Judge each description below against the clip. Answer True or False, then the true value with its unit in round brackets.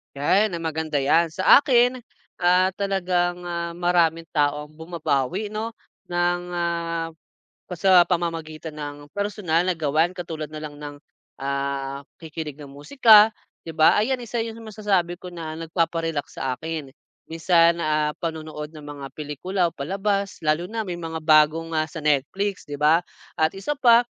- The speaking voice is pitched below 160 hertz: False (165 Hz)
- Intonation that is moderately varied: True (3.4 semitones)